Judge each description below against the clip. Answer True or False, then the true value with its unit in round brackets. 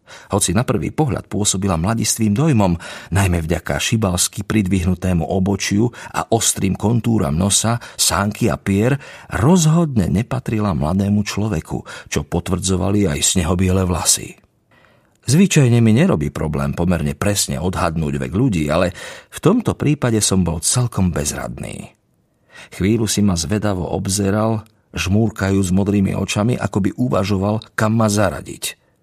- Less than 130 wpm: True (120 wpm)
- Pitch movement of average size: True (3.3 semitones)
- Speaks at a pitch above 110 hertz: False (100 Hz)